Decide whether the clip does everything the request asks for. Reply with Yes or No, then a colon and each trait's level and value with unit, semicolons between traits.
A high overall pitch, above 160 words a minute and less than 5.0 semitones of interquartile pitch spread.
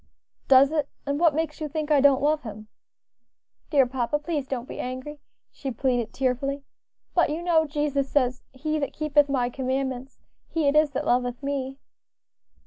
Yes: very high, 280 Hz; average, 170 wpm; narrow, 2.6 semitones